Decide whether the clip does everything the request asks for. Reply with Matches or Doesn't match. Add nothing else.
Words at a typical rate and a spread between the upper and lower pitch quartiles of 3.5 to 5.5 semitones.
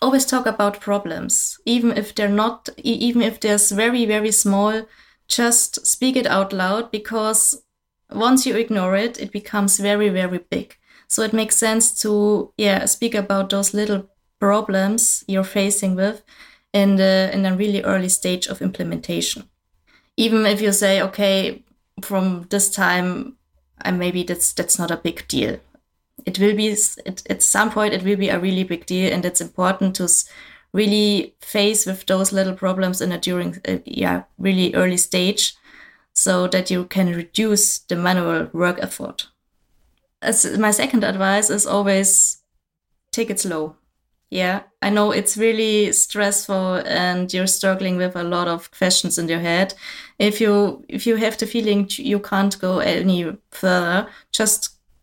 Doesn't match